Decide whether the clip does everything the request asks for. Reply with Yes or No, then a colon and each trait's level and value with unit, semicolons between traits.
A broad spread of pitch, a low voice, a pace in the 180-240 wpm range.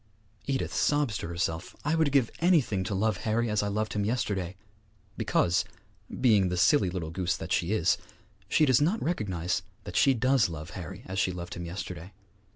Yes: wide, 6.1 semitones; low, 100 Hz; average, 185 wpm